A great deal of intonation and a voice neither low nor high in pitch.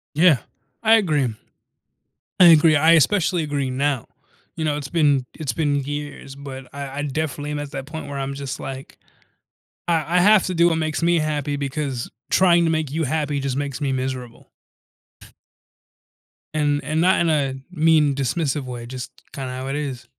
No: average, 2.8 semitones; medium, 145 Hz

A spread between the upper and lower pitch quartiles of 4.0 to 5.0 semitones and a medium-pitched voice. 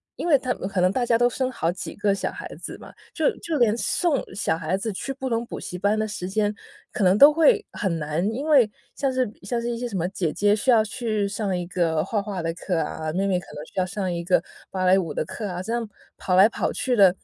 No: average, 4.6 semitones; high, 205 Hz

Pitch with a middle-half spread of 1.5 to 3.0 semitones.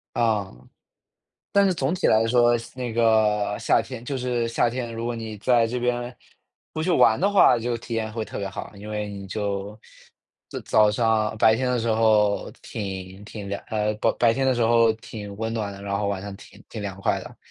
Yes: narrow, 2.5 semitones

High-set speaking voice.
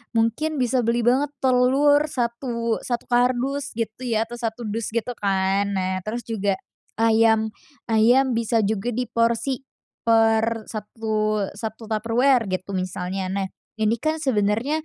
Yes: high, 230 Hz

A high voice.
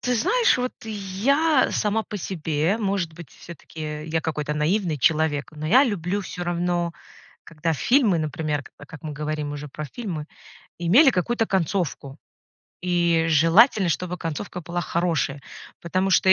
No: medium, 170 Hz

